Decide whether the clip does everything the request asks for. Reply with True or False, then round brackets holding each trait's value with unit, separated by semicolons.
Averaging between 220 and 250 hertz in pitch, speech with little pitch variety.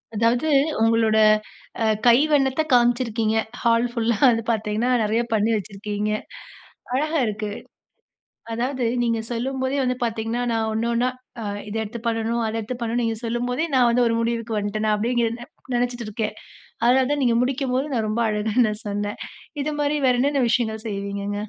True (230 Hz; 2.3 semitones)